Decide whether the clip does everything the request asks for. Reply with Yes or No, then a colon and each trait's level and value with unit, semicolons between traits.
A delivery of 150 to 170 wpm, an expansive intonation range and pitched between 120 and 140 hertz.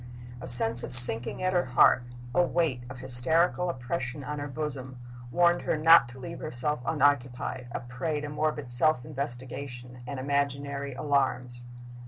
No: average, 155 wpm; average, 3.3 semitones; low, 135 Hz